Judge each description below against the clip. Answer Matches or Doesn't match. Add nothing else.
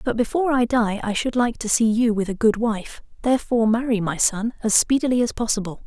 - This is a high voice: Matches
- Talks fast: Matches